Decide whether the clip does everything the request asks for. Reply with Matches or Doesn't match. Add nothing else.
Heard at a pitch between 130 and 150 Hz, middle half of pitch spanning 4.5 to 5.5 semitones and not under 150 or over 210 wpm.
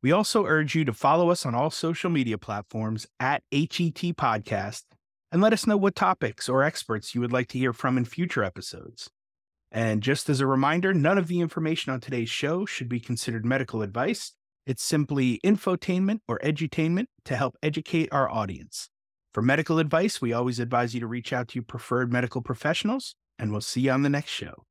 Matches